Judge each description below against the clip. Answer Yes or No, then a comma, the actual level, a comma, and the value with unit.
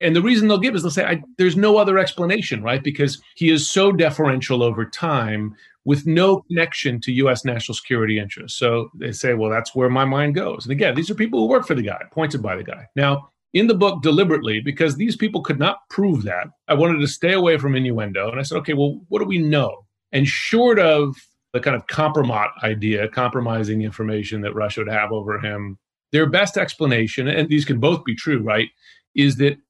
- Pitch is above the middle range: No, medium, 140 Hz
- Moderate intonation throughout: No, wide, 6.3 semitones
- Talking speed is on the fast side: Yes, fast, 220 wpm